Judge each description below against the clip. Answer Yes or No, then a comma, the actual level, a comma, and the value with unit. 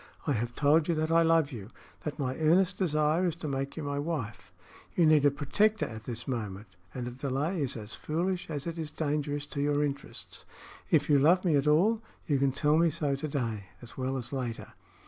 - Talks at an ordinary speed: No, fast, 220 wpm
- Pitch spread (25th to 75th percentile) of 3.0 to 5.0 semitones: Yes, average, 3.4 semitones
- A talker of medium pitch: Yes, medium, 145 Hz